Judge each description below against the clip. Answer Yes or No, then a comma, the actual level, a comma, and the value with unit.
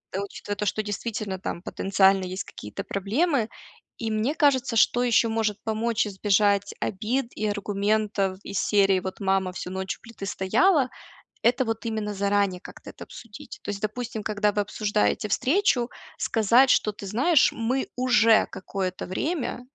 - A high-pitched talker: Yes, high, 210 Hz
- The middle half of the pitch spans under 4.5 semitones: Yes, average, 3.0 semitones